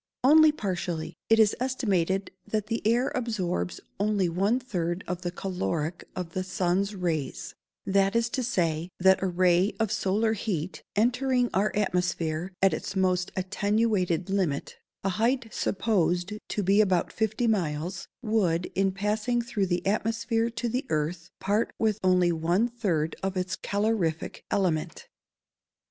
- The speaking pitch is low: No, high, 195 Hz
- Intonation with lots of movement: No, average, 3.8 semitones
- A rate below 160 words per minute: Yes, average, 150 wpm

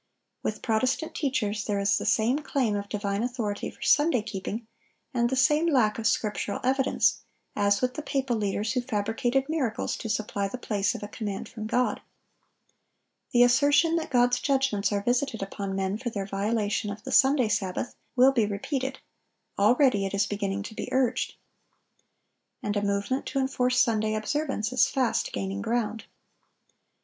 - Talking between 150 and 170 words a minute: Yes, average, 165 wpm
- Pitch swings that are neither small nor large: Yes, average, 4.2 semitones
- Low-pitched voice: No, high, 225 Hz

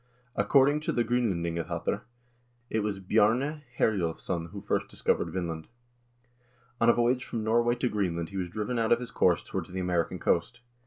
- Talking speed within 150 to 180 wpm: Yes, average, 170 wpm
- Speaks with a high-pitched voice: No, low, 110 Hz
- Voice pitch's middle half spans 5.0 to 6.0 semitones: Yes, average, 5.3 semitones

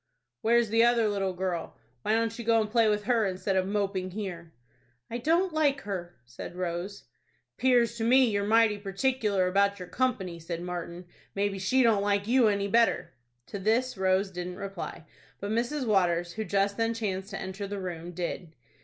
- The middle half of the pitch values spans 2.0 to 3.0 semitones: No, average, 3.6 semitones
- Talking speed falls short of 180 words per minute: No, average, 185 wpm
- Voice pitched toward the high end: Yes, high, 200 Hz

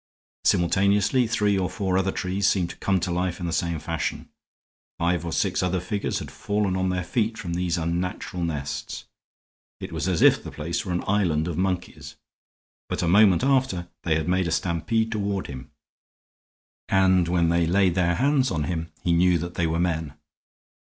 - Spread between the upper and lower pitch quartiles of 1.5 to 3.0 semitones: Yes, narrow, 2.4 semitones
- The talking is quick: No, average, 185 wpm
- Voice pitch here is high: No, very low, 90 Hz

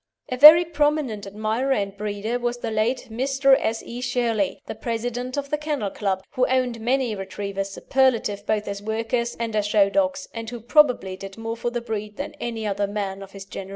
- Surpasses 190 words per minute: Yes, average, 200 wpm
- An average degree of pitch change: Yes, average, 3.8 semitones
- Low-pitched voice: No, high, 230 Hz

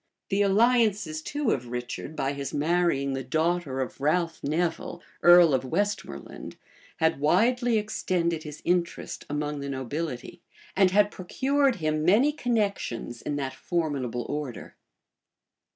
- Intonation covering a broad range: Yes, wide, 6.1 semitones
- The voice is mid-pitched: Yes, medium, 165 Hz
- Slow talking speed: Yes, slow, 130 wpm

